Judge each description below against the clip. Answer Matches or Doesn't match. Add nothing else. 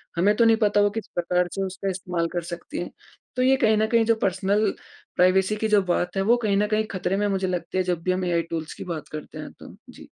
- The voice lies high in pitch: Matches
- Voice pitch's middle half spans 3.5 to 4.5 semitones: Doesn't match